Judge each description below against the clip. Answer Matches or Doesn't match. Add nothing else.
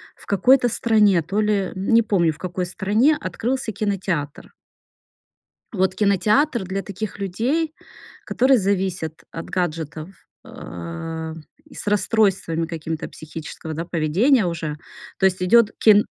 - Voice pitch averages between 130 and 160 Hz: Doesn't match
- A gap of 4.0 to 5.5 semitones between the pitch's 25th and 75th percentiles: Matches